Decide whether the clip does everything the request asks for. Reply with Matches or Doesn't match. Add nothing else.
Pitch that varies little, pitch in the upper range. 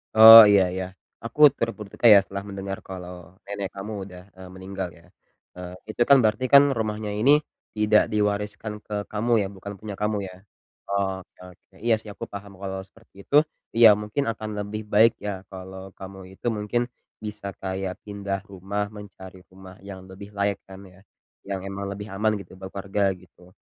Doesn't match